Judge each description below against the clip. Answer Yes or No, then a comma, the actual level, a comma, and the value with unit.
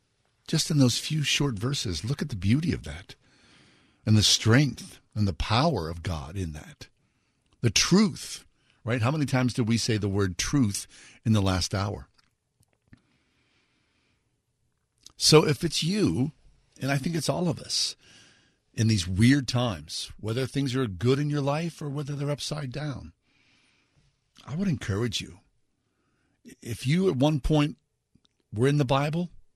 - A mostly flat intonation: No, average, 4.9 semitones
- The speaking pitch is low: Yes, low, 130 Hz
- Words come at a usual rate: Yes, average, 160 wpm